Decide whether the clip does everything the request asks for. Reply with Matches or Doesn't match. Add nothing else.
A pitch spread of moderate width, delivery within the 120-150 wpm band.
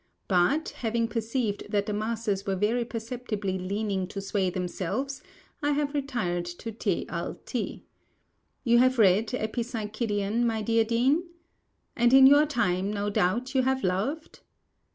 Matches